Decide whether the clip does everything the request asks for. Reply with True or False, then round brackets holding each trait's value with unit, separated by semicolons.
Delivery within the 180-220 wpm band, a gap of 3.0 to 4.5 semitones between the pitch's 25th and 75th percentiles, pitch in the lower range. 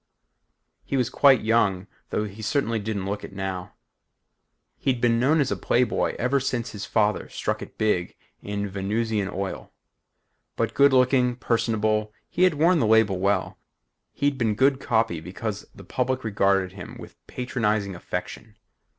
False (155 wpm; 4.0 semitones; 110 Hz)